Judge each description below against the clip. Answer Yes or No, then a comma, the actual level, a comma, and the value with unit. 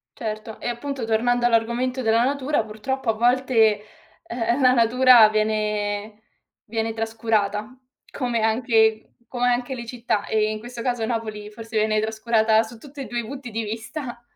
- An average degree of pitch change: No, narrow, 2.0 semitones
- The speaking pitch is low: No, high, 225 Hz